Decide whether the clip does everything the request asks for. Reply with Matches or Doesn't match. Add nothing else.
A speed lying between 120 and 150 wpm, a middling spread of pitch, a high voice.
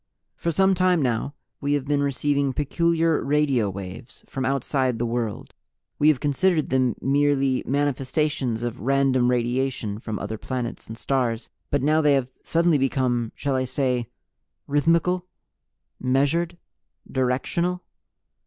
Doesn't match